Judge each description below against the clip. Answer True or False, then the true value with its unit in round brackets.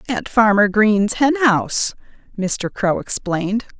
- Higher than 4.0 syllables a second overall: False (3.9 syllables/s)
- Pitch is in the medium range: False (215 Hz)